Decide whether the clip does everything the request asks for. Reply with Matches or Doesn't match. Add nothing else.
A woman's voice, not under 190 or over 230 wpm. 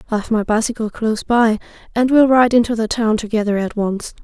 Matches